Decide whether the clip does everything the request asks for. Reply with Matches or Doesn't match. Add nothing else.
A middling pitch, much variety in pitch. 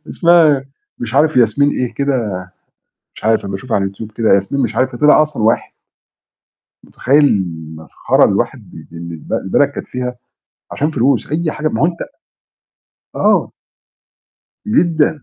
Doesn't match